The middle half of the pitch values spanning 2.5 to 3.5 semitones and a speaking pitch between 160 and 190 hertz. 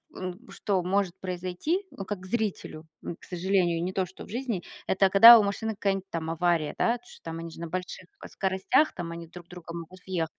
Yes: average, 2.8 semitones; medium, 185 Hz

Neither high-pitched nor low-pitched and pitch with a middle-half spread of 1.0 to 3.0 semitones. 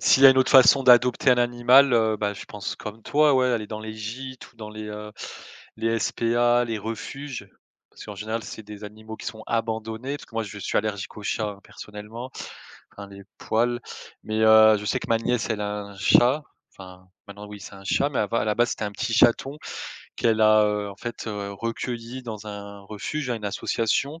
No: low, 110 Hz; narrow, 2.5 semitones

